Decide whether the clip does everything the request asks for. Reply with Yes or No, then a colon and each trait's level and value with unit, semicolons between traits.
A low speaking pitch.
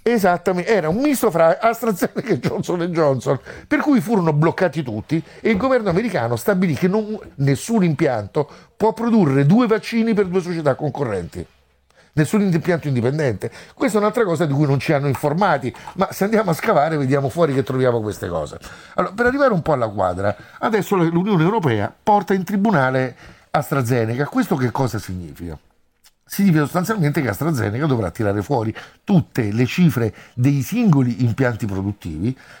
No: medium, 160 Hz